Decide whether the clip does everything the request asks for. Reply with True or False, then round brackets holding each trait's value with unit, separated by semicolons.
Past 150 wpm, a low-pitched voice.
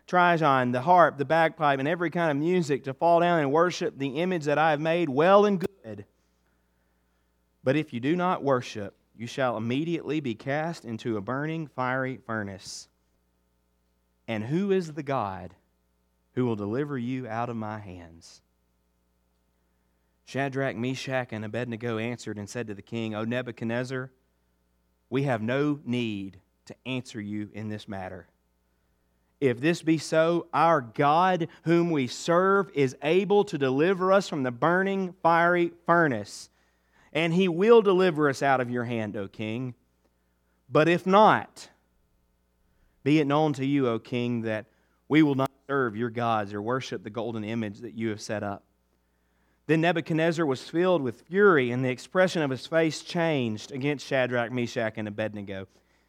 True (160 wpm; 125 Hz)